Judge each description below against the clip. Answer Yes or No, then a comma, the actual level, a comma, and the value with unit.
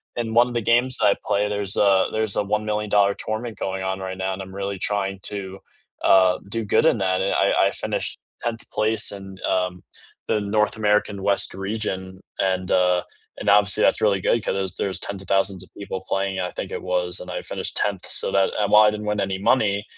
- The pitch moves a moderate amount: No, narrow, 1.9 semitones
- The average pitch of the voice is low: Yes, low, 100 Hz